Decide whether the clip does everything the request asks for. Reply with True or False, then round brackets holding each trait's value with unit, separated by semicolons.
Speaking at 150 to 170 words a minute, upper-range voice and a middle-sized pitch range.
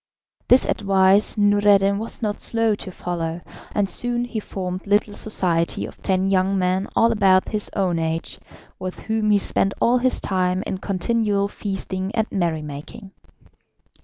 False (155 wpm; 195 Hz; 2.3 semitones)